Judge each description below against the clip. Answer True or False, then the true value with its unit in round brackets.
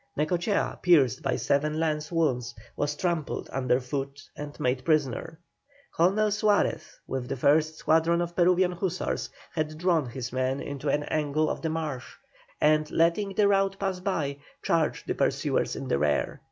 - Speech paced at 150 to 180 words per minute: True (160 wpm)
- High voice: False (155 Hz)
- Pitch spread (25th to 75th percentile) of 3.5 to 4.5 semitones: True (3.9 semitones)